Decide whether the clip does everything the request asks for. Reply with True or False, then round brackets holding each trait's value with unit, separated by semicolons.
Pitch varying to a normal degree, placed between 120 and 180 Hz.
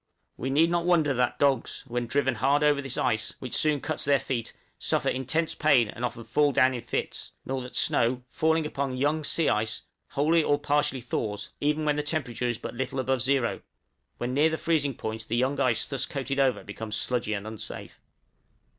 True (3.4 semitones; 135 Hz)